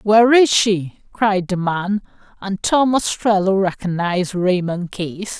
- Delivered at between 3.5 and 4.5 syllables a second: Yes, 3.9 syllables/s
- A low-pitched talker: No, high, 195 Hz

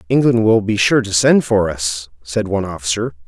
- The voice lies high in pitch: No, low, 105 Hz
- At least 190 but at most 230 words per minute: Yes, average, 200 wpm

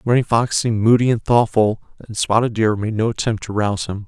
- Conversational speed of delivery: No, fast, 220 wpm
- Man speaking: Yes, male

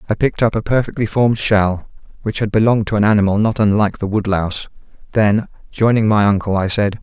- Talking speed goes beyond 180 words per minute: Yes, average, 195 wpm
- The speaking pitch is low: Yes, low, 105 Hz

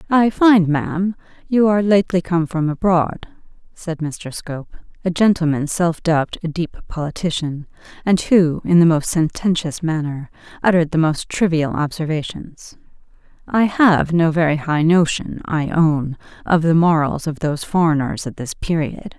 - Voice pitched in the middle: Yes, medium, 165 Hz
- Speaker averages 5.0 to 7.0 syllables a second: No, 4.7 syllables/s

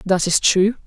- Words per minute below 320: Yes, fast, 210 wpm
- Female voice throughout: Yes, female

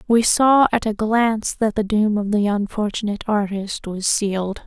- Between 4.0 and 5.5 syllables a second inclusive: Yes, 4.8 syllables/s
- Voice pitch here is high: Yes, high, 210 Hz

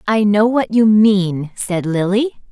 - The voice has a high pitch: Yes, high, 205 Hz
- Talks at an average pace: Yes, average, 165 wpm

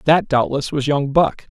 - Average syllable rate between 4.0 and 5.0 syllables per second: Yes, 4.4 syllables/s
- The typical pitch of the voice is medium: Yes, medium, 145 Hz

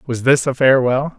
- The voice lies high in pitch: No, low, 130 Hz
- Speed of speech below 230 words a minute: Yes, average, 200 wpm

